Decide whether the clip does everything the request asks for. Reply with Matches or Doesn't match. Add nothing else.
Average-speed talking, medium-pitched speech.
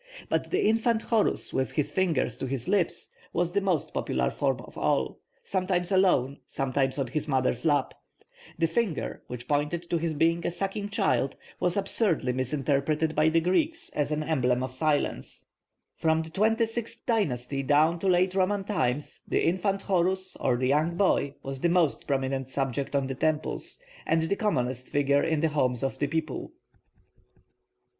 Matches